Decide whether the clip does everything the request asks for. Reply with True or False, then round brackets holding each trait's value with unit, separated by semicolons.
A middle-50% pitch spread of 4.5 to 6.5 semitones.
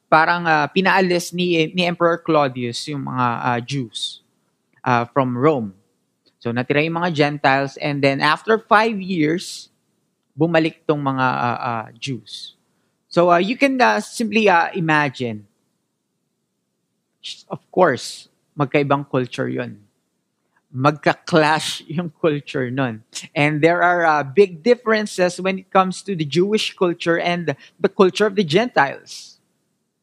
True (4.8 semitones)